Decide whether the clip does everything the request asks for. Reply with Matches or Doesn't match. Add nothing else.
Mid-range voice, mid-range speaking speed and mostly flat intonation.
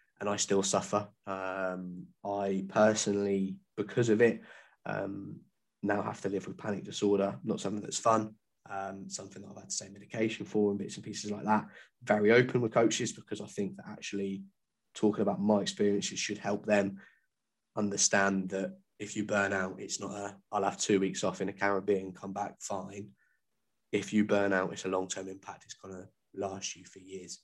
Doesn't match